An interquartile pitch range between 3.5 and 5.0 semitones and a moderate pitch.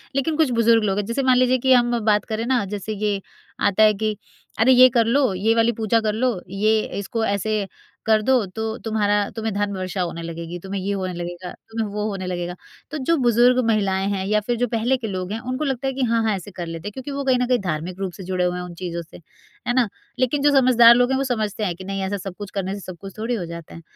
No: average, 4.2 semitones; high, 215 Hz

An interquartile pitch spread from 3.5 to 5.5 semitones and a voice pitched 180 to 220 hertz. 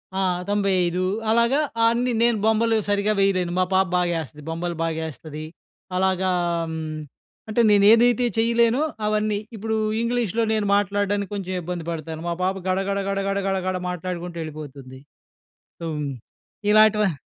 Yes: average, 3.8 semitones; high, 195 Hz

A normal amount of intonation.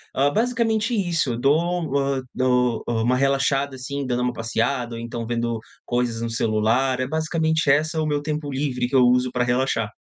Yes: average, 3.6 semitones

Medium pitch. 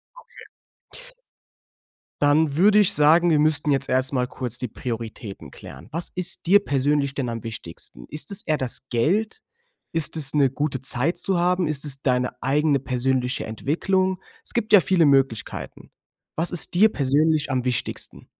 Yes: medium, 145 Hz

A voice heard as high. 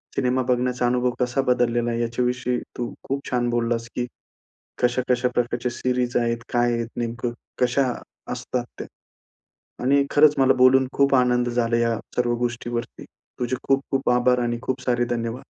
No: low, 125 Hz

